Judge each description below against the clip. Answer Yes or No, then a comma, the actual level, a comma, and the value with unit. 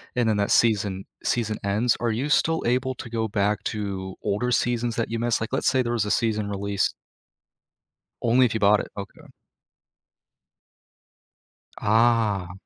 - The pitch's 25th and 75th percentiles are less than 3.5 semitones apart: Yes, average, 2.7 semitones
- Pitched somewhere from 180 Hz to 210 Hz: No, low, 110 Hz